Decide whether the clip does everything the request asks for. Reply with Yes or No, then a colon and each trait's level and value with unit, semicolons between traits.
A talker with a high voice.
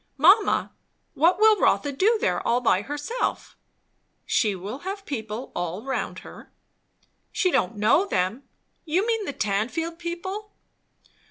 Yes: very high, 290 Hz